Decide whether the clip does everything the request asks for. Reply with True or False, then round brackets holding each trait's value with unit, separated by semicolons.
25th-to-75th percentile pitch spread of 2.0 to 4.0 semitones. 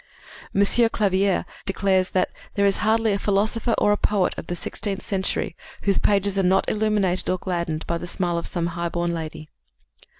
True (2.7 semitones)